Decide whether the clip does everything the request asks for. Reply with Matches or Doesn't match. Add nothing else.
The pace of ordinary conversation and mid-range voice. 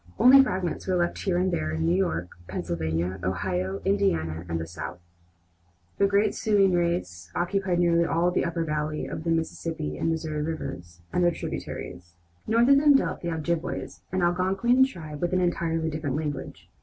Matches